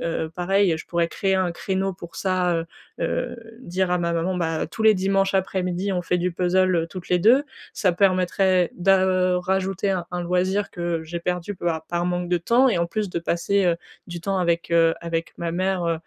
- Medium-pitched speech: Yes, medium, 180 Hz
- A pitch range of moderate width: No, narrow, 2.0 semitones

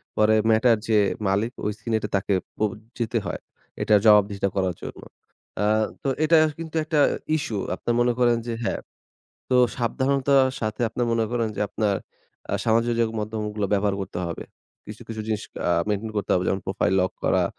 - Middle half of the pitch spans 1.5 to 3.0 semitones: Yes, average, 2.7 semitones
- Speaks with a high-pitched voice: No, low, 110 Hz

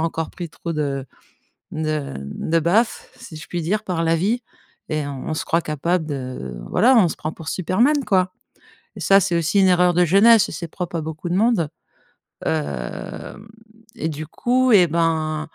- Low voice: No, medium, 165 Hz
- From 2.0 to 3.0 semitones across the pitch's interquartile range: No, average, 3.5 semitones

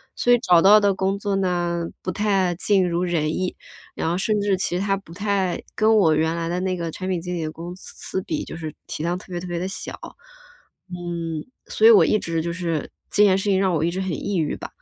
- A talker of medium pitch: Yes, medium, 180 Hz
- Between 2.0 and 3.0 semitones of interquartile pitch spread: Yes, narrow, 2.5 semitones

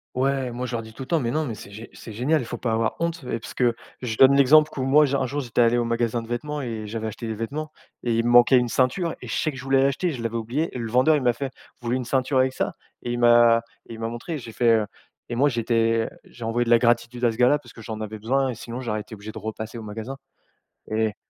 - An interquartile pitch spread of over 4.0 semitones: No, average, 2.7 semitones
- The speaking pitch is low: Yes, low, 120 Hz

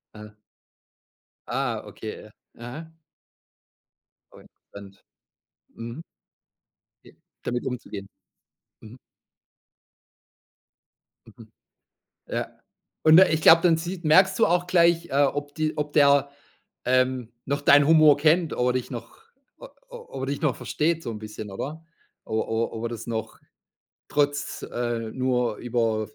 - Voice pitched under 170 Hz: Yes, medium, 140 Hz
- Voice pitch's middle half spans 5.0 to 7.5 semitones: Yes, average, 5.3 semitones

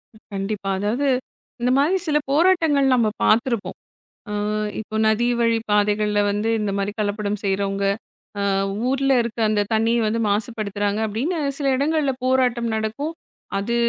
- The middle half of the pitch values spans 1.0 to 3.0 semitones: No, average, 4.2 semitones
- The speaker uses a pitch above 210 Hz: Yes, high, 225 Hz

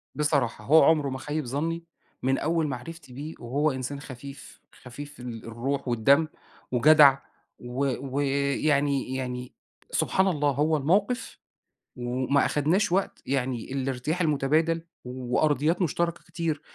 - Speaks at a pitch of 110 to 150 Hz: Yes, medium, 140 Hz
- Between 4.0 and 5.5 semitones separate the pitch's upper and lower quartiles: No, average, 3.5 semitones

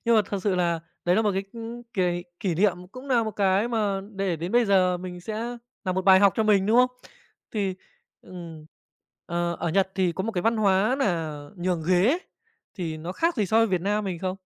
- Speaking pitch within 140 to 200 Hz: Yes, high, 195 Hz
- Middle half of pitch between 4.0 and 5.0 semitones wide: No, average, 3.5 semitones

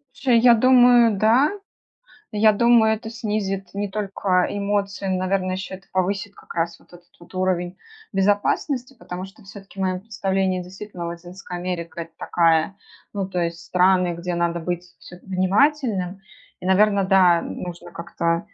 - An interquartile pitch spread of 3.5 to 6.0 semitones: No, narrow, 2.6 semitones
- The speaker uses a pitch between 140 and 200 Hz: Yes, high, 190 Hz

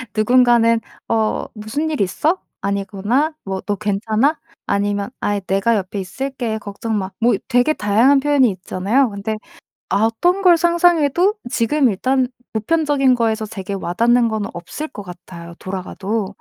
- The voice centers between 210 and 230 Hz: Yes, high, 225 Hz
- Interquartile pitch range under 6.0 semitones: Yes, average, 5.1 semitones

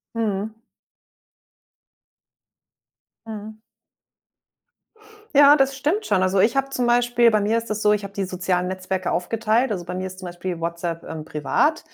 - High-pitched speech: Yes, high, 210 Hz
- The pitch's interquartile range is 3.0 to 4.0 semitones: No, average, 4.5 semitones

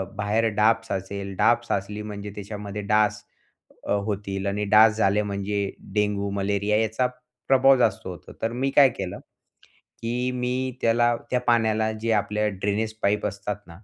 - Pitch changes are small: Yes, narrow, 2.2 semitones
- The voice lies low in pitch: Yes, low, 105 Hz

